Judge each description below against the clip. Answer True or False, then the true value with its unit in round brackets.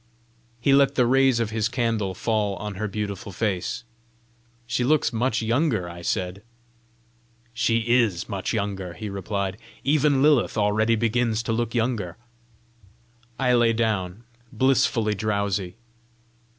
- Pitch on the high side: False (110 Hz)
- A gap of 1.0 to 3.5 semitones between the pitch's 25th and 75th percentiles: True (3.1 semitones)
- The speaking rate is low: True (130 wpm)